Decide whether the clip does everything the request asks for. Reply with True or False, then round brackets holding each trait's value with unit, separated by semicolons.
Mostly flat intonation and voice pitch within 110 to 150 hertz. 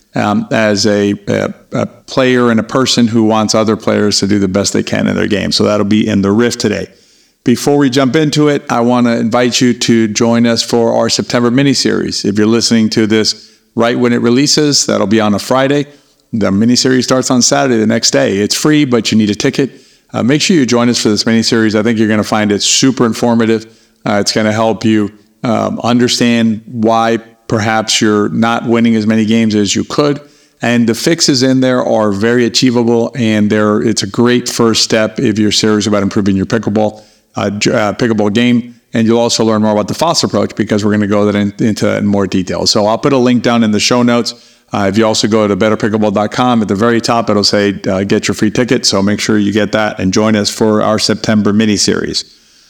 True (2.3 semitones; 115 Hz)